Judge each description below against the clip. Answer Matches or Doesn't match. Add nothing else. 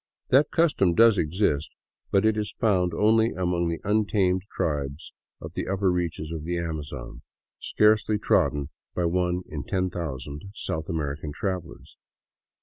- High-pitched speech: Doesn't match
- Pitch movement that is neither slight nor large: Matches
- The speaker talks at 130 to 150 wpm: Matches